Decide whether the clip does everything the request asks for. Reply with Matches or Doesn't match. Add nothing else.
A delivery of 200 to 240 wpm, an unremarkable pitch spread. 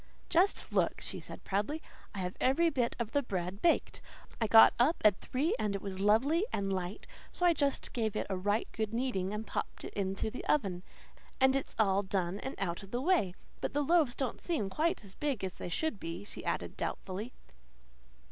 Doesn't match